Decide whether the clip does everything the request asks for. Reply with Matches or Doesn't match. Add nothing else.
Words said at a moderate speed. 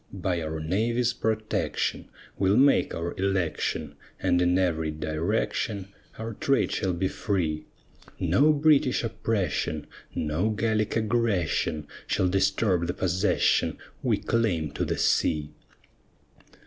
Doesn't match